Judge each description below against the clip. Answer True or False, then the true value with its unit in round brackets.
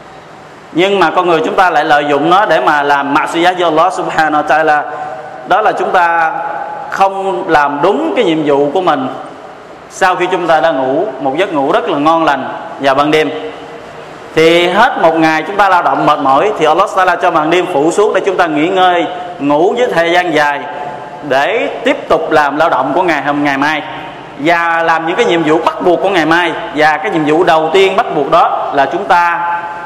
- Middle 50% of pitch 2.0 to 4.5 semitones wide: True (3.1 semitones)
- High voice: False (160 Hz)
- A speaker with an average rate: True (215 wpm)